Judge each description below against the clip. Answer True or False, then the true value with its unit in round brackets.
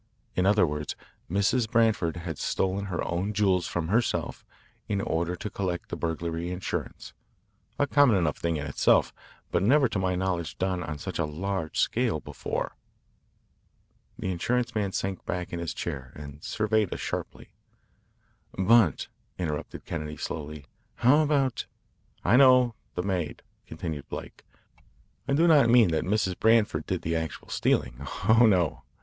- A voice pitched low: True (95 Hz)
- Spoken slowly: False (155 wpm)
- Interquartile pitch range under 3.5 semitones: False (5.0 semitones)